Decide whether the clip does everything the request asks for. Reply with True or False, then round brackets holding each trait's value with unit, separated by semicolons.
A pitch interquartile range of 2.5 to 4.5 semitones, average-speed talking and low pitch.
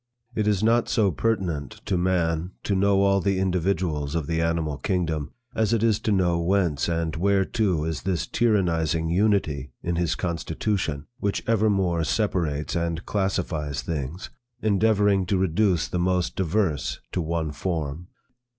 True (3.5 semitones; 150 wpm; 90 Hz)